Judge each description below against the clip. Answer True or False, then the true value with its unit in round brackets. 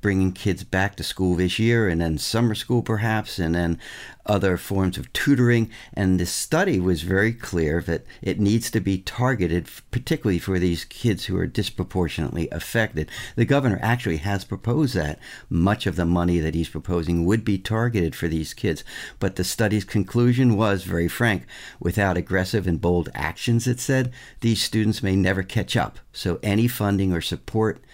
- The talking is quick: False (175 wpm)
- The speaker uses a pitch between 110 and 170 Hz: False (95 Hz)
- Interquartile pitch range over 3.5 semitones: True (4.3 semitones)